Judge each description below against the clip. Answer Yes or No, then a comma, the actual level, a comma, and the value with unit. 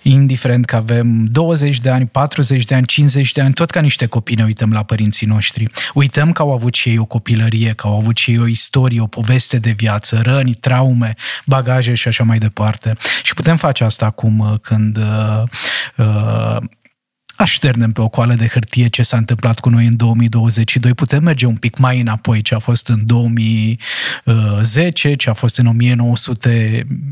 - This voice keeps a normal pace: No, fast, 185 wpm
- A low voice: Yes, low, 120 Hz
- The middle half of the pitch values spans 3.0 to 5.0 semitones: No, narrow, 2.4 semitones